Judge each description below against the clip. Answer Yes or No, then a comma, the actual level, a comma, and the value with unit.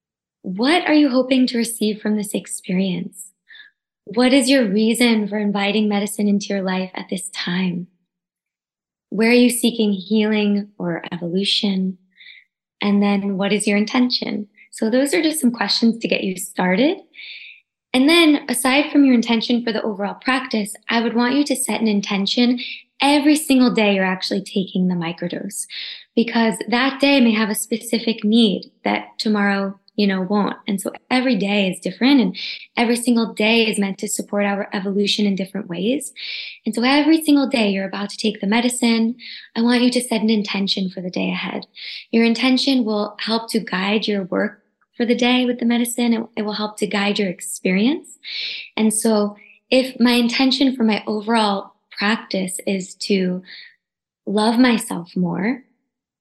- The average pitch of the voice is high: Yes, high, 220 Hz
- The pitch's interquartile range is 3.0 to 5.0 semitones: Yes, average, 3.6 semitones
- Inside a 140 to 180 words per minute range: Yes, average, 170 wpm